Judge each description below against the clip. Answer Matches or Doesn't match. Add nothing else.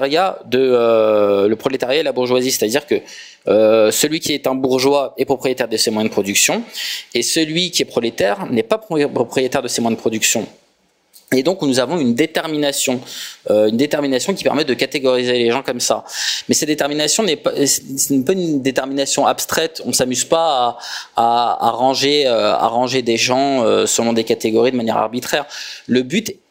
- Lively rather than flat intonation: Doesn't match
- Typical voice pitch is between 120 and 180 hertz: Matches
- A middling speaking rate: Matches